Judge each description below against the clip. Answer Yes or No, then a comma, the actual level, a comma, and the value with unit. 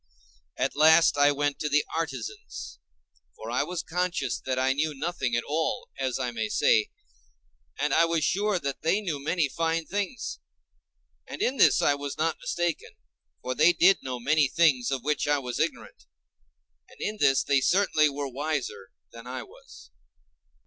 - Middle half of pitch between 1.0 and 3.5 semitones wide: No, average, 4.1 semitones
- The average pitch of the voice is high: No, medium, 150 Hz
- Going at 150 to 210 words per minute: Yes, average, 170 wpm